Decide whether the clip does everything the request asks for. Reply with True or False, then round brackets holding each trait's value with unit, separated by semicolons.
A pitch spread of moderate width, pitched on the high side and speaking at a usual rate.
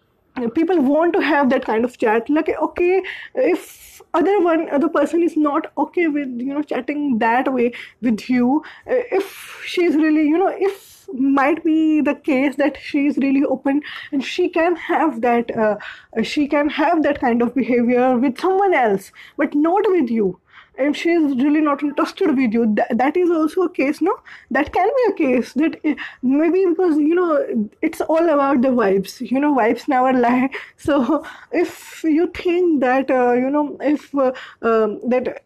True (4.7 semitones; 295 Hz; 180 wpm)